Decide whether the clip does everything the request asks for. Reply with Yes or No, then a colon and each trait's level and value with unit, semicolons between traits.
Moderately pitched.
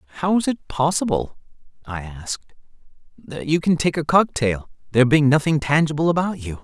Yes: medium, 145 Hz